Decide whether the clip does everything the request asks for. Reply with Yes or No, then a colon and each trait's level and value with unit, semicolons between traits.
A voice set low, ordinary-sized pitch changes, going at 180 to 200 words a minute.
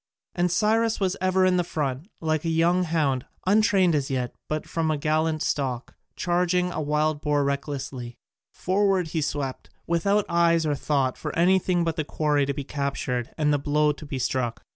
No: medium, 155 Hz; average, 3.9 semitones; average, 185 wpm